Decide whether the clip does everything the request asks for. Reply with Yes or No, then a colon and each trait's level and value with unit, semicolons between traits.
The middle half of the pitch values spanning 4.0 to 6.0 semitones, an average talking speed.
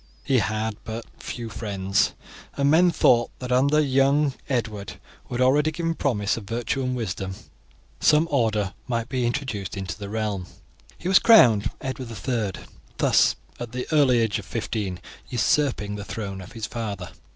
Yes: average, 4.5 semitones; average, 165 wpm